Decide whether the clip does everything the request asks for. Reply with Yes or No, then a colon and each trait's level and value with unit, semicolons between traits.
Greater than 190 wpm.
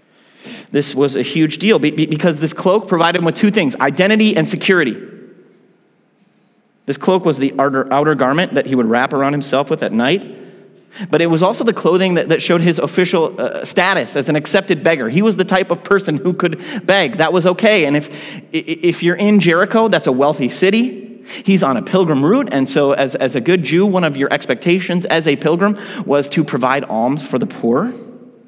Yes: average, 200 wpm